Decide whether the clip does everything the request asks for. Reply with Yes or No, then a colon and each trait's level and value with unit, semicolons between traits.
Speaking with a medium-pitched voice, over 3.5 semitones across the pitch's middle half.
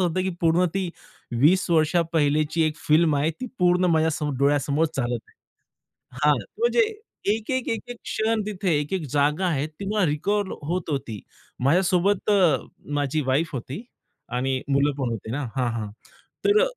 Yes: medium, 155 Hz; average, 4.6 semitones